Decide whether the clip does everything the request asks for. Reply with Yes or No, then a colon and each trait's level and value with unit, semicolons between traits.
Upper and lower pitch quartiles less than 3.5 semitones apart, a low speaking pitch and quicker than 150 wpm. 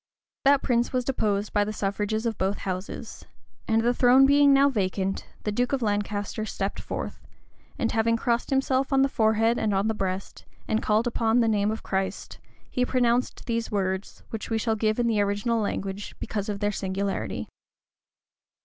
No: average, 3.0 semitones; high, 220 Hz; average, 180 wpm